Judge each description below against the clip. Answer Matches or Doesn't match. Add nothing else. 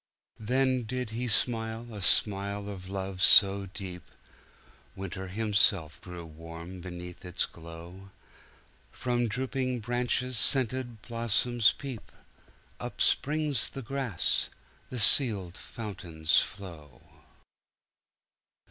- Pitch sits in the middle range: Doesn't match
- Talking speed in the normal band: Doesn't match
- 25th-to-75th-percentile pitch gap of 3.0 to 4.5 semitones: Doesn't match